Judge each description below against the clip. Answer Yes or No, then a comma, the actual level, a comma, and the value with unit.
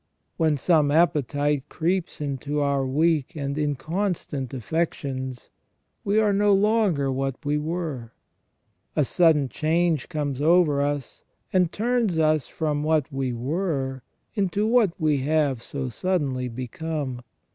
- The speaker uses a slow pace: Yes, slow, 130 wpm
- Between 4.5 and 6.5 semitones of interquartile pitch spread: No, average, 4.0 semitones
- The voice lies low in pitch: No, medium, 150 Hz